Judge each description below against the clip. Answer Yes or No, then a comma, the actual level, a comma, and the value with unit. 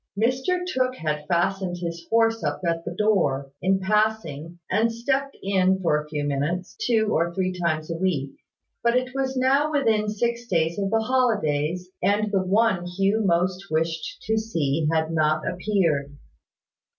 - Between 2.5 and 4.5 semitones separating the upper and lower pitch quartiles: No, wide, 5.4 semitones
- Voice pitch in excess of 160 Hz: Yes, high, 190 Hz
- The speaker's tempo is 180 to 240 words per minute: No, average, 160 wpm